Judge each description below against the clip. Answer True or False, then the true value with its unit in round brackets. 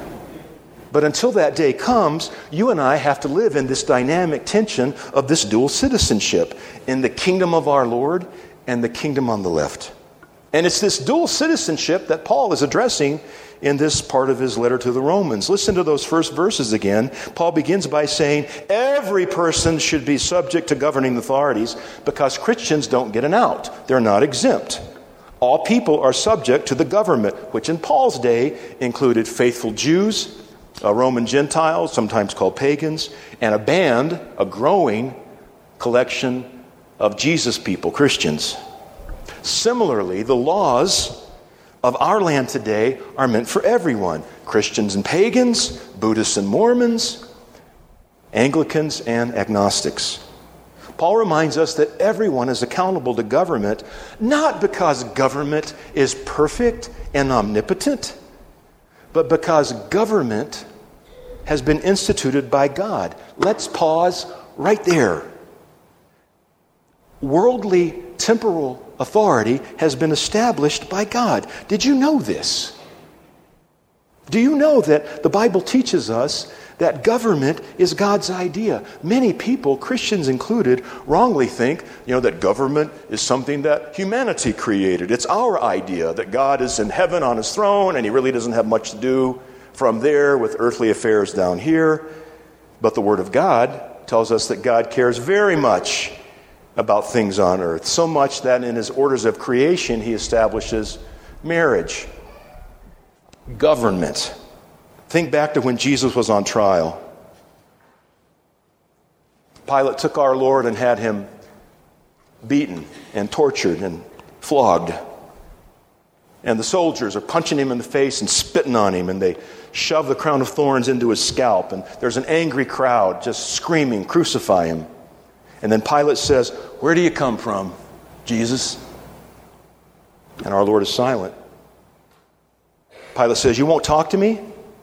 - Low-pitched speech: False (150 Hz)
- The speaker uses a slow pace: False (145 wpm)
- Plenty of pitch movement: True (7.4 semitones)